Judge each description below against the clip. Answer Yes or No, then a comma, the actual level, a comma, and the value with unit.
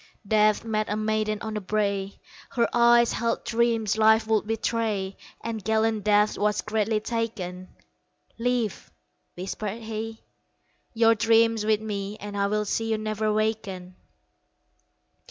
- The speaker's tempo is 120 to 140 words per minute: Yes, slow, 135 wpm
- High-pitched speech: Yes, high, 215 Hz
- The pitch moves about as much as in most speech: No, narrow, 1.4 semitones